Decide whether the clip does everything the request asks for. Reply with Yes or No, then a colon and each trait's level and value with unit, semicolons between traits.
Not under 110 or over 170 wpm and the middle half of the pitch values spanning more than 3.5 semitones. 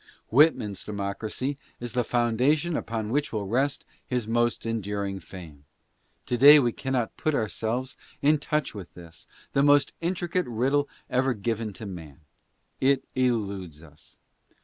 Yes: average, 140 wpm; average, 5.3 semitones